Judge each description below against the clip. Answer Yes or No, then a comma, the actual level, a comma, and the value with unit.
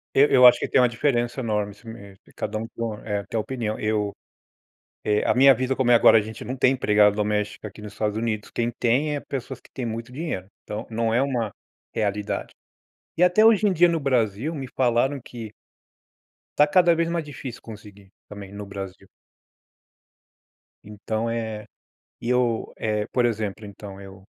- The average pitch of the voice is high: No, low, 115 Hz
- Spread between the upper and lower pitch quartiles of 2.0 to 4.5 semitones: Yes, average, 3.7 semitones